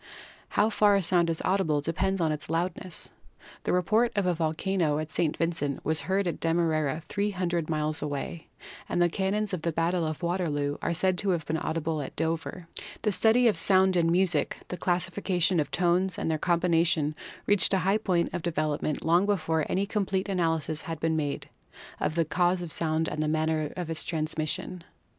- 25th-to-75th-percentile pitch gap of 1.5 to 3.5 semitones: Yes, average, 2.9 semitones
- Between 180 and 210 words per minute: Yes, average, 190 wpm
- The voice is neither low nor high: Yes, medium, 170 Hz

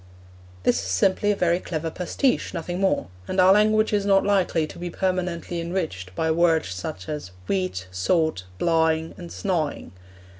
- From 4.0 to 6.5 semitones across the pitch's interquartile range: No, average, 3.4 semitones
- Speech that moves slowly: No, average, 160 wpm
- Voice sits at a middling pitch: Yes, medium, 170 Hz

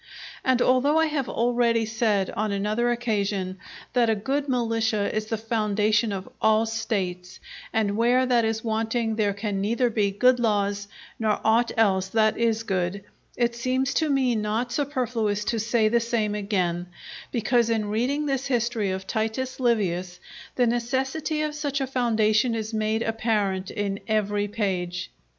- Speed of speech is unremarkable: Yes, average, 160 wpm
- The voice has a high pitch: Yes, high, 225 Hz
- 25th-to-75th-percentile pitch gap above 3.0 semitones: No, average, 2.7 semitones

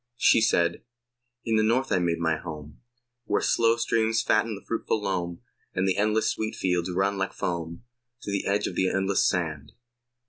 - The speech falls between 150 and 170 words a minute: No, average, 180 wpm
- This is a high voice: No, very low, 95 Hz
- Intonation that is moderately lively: Yes, average, 4.0 semitones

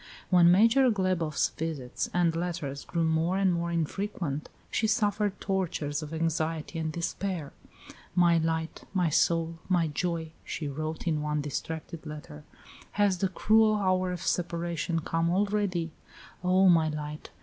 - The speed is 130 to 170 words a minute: Yes, average, 140 wpm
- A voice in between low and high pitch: Yes, medium, 170 Hz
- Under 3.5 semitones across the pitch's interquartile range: Yes, average, 2.8 semitones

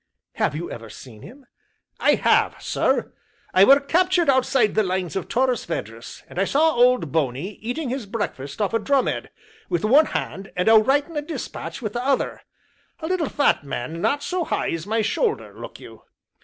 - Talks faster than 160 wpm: Yes, average, 190 wpm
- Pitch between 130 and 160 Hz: No, high, 230 Hz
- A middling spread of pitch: No, wide, 8.1 semitones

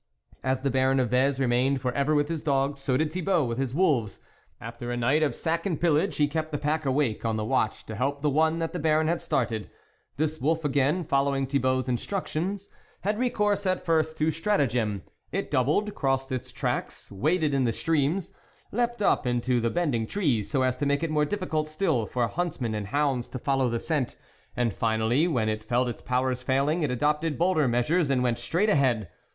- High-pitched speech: No, medium, 140 Hz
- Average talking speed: No, fast, 215 wpm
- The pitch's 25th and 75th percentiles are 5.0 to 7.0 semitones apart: No, average, 4.2 semitones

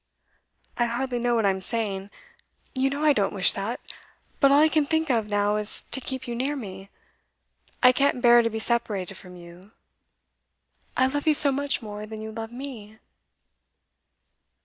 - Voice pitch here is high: Yes, high, 235 Hz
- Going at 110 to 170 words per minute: No, average, 180 wpm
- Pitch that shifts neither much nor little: Yes, average, 4.4 semitones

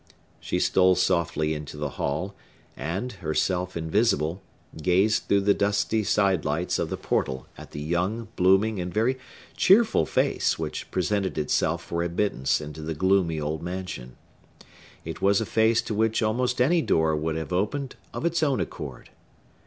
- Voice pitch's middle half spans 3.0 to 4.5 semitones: No, average, 5.3 semitones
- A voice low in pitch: Yes, very low, 90 Hz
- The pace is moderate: Yes, average, 160 wpm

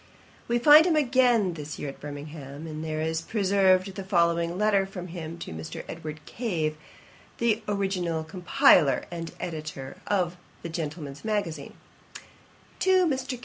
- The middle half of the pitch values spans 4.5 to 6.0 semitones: Yes, average, 4.8 semitones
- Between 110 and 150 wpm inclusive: Yes, average, 145 wpm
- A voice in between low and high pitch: Yes, medium, 175 Hz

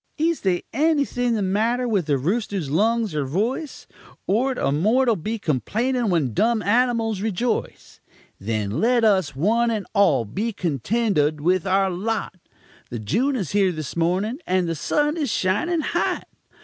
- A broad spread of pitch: Yes, wide, 5.8 semitones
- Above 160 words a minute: No, average, 155 wpm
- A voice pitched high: Yes, high, 205 Hz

